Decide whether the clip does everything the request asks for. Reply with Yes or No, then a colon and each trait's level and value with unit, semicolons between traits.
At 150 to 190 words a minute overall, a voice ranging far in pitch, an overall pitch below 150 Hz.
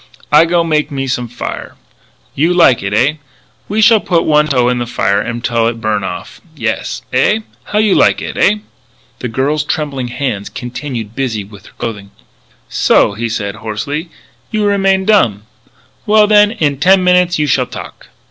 Yes: average, 175 wpm; wide, 7.7 semitones; medium, 140 Hz